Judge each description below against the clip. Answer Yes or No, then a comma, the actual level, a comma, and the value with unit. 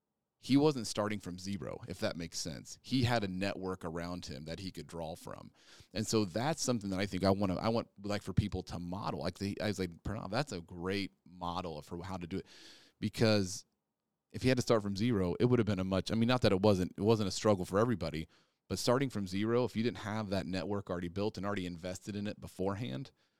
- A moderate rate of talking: No, fast, 245 wpm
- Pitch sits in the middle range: No, low, 100 Hz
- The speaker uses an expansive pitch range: No, average, 3.3 semitones